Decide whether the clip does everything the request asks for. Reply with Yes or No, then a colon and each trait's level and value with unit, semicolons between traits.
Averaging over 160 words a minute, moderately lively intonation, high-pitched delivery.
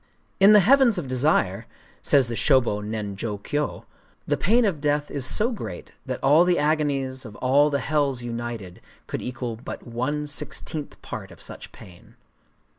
No: average, 170 wpm; average, 4.3 semitones; low, 135 Hz